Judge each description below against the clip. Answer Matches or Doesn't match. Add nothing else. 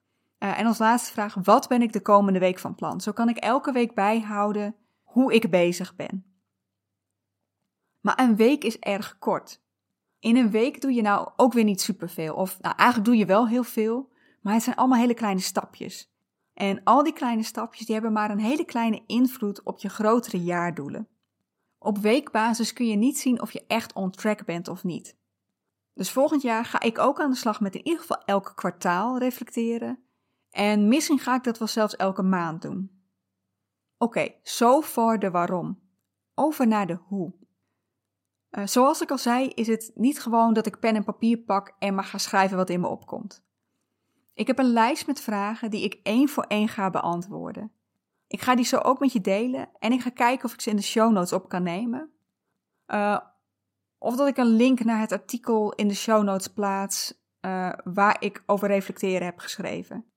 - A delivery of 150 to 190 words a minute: Doesn't match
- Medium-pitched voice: Doesn't match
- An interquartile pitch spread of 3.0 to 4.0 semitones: Matches